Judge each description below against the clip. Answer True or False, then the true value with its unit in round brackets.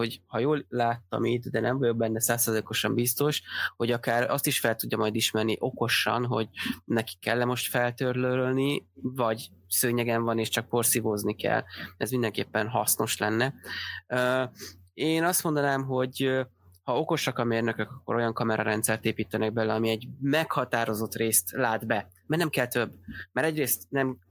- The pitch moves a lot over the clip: False (2.7 semitones)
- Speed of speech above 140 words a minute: True (155 wpm)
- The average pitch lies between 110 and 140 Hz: True (120 Hz)